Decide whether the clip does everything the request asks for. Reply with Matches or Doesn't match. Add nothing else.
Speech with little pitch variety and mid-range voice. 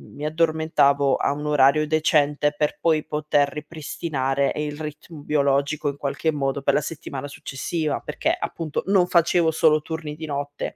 Matches